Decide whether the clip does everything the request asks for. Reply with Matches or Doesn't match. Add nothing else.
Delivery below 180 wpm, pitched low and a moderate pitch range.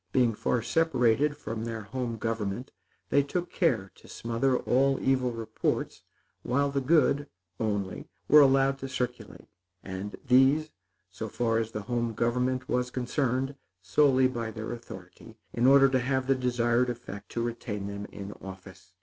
Matches